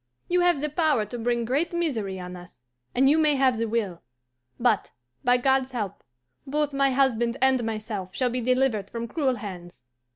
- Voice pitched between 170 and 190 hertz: No, high, 245 Hz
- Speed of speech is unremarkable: Yes, average, 185 wpm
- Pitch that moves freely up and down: No, average, 4.1 semitones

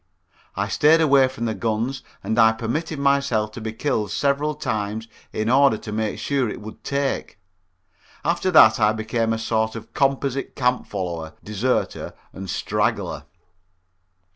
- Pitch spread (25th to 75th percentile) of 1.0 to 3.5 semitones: No, average, 4.2 semitones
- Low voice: Yes, low, 115 Hz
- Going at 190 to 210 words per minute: No, average, 150 wpm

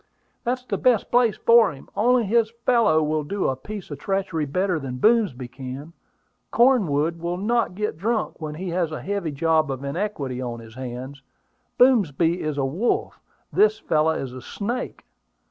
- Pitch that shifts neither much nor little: No, wide, 7.3 semitones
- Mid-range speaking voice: Yes, medium, 170 Hz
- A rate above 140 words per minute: Yes, average, 170 wpm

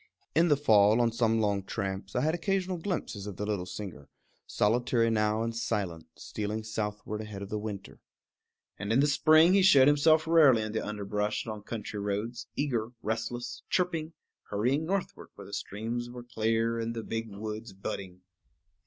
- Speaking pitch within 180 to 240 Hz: No, low, 115 Hz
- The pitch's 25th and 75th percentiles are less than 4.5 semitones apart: Yes, average, 3.9 semitones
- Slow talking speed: No, average, 170 wpm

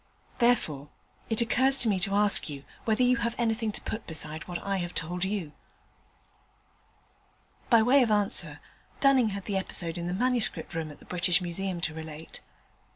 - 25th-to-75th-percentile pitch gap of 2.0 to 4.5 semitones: No, average, 5.2 semitones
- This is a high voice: Yes, high, 195 Hz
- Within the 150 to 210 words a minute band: Yes, average, 175 wpm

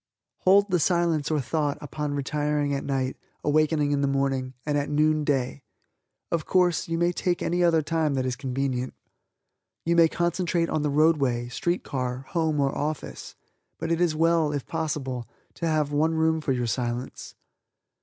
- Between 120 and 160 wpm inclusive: No, average, 175 wpm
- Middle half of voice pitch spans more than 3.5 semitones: No, average, 3.1 semitones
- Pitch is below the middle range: No, medium, 150 Hz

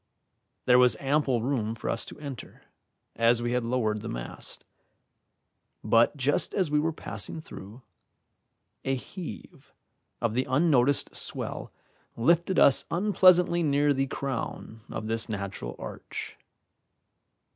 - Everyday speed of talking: No, slow, 125 wpm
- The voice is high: No, low, 130 Hz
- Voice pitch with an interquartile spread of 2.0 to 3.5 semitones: No, average, 4.6 semitones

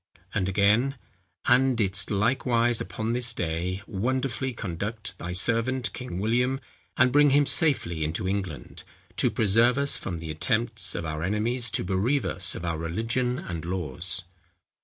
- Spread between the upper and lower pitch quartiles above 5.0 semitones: Yes, wide, 5.6 semitones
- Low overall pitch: Yes, low, 110 Hz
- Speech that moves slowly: No, average, 150 wpm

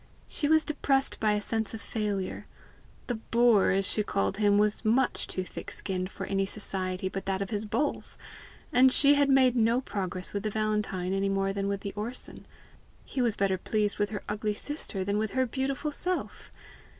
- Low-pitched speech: No, high, 210 Hz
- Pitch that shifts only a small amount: No, average, 3.8 semitones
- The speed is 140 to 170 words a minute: No, average, 195 wpm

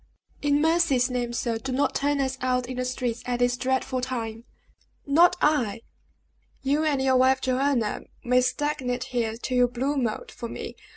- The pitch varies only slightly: Yes, narrow, 2.0 semitones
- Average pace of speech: Yes, average, 175 wpm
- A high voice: Yes, very high, 255 Hz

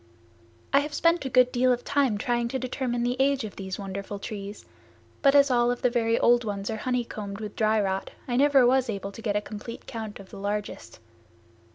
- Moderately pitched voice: No, high, 235 Hz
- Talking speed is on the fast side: Yes, fast, 220 wpm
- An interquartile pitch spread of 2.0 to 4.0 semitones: Yes, average, 3.7 semitones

